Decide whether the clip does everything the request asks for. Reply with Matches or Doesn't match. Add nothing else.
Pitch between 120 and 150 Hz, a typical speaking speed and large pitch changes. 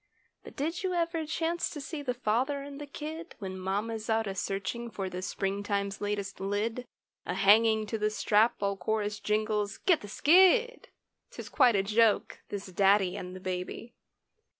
Doesn't match